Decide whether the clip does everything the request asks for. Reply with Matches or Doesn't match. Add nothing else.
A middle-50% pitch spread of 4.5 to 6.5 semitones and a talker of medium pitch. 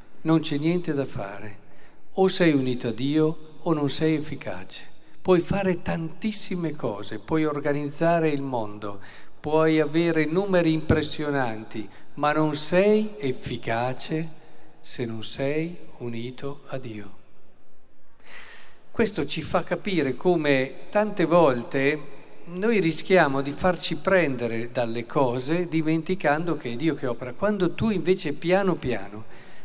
Matches